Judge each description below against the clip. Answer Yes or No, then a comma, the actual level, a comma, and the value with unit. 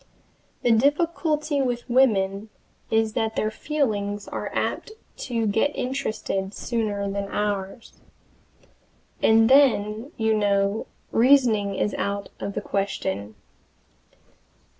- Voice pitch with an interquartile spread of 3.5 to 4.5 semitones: Yes, average, 3.9 semitones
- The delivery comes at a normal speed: No, slow, 105 wpm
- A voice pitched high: Yes, high, 220 Hz